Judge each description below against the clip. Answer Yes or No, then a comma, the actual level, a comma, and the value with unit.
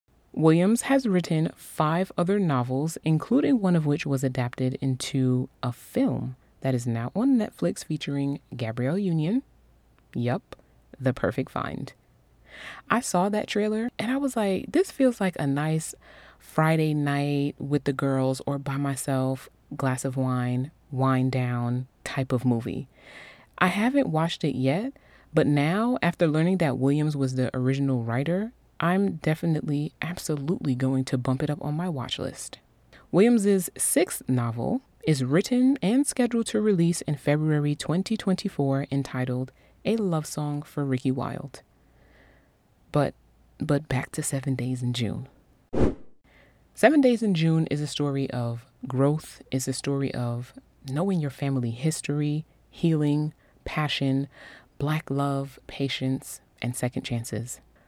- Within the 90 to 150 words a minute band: Yes, average, 140 wpm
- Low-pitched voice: No, medium, 145 Hz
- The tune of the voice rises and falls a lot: No, average, 4.9 semitones